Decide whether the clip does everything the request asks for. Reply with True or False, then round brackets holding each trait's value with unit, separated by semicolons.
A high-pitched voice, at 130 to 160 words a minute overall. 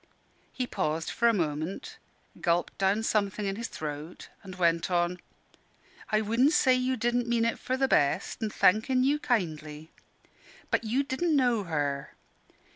True (215 Hz; 155 wpm)